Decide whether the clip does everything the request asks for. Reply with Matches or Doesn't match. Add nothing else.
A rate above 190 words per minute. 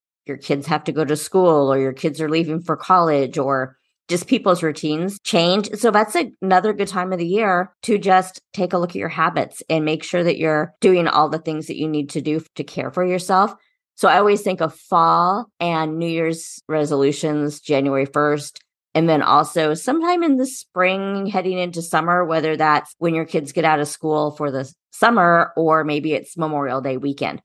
Matches